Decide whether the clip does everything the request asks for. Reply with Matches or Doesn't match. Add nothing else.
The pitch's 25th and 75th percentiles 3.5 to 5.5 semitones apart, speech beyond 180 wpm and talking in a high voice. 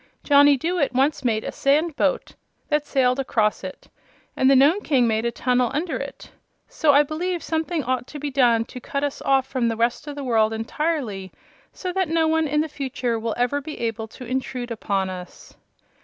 Matches